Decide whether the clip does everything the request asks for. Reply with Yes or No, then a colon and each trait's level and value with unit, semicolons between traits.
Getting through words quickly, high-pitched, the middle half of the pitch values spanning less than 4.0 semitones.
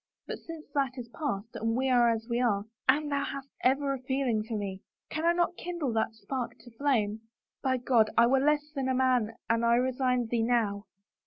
Yes: fast, 220 wpm; very high, 250 Hz; average, 3.3 semitones